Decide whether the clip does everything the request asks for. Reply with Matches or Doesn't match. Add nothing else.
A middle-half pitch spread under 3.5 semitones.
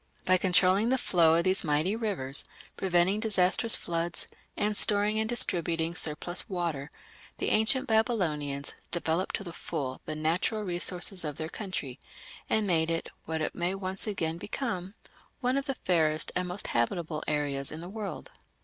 Doesn't match